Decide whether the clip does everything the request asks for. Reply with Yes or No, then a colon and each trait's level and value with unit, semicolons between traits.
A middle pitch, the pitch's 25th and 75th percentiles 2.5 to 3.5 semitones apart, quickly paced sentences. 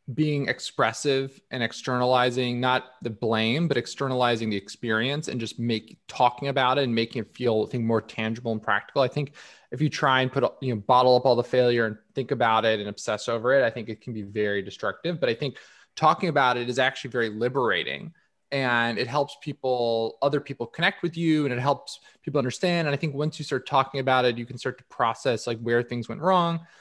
No: low, 125 Hz; average, 3.2 semitones; fast, 220 wpm